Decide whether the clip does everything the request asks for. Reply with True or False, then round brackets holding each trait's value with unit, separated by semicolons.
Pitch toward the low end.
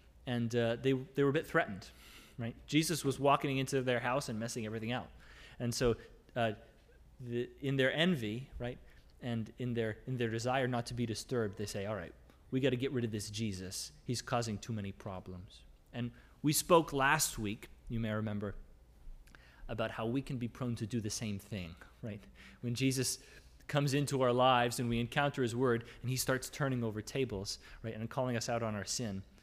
True (120 Hz)